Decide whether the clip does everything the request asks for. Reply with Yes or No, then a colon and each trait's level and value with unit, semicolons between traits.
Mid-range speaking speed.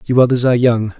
No: fast, 240 wpm